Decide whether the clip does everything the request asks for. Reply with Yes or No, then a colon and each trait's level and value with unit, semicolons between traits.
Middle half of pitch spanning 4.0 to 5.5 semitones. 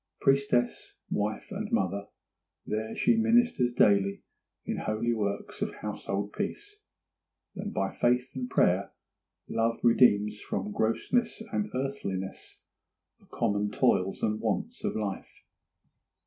Yes: average, 5.1 semitones